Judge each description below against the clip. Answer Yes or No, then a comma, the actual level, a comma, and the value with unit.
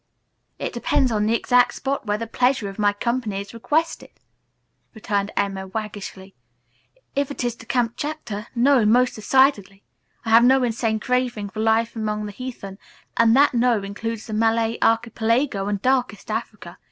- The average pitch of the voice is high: Yes, high, 225 Hz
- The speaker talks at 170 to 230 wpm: No, average, 160 wpm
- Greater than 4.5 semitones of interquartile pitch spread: No, average, 3.1 semitones